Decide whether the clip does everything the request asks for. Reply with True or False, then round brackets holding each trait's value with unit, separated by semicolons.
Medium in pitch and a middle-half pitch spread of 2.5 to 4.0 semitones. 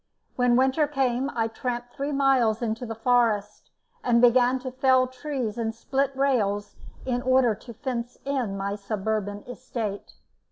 False (245 Hz; 2.8 semitones)